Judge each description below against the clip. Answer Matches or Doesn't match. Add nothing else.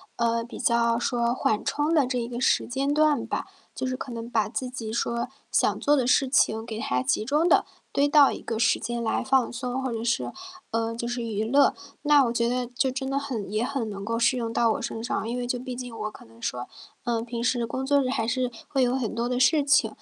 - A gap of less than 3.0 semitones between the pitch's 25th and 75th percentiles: Matches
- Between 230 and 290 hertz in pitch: Matches